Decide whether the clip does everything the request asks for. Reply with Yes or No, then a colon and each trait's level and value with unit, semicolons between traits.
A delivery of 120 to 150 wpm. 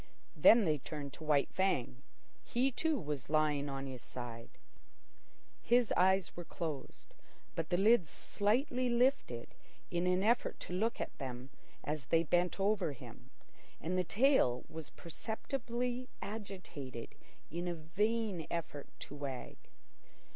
Yes: slow, 135 wpm